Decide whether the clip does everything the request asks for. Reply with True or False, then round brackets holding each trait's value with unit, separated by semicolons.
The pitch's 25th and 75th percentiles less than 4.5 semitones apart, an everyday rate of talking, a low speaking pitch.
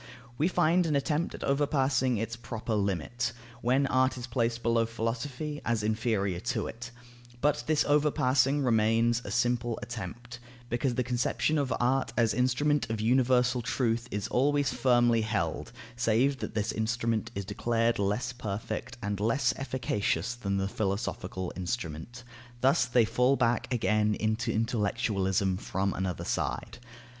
True (3.0 semitones; 145 wpm; 120 Hz)